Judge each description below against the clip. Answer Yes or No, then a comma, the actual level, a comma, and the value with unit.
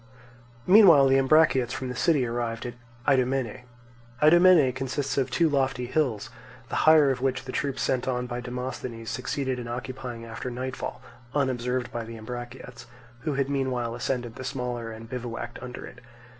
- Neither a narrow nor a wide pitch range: No, narrow, 1.8 semitones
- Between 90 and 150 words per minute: No, average, 160 wpm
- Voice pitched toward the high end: No, low, 125 Hz